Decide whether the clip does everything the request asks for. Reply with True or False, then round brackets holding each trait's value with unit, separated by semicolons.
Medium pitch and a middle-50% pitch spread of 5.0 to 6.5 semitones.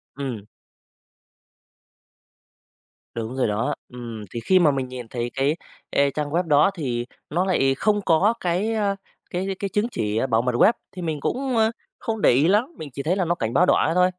False (155 Hz; 7.2 semitones)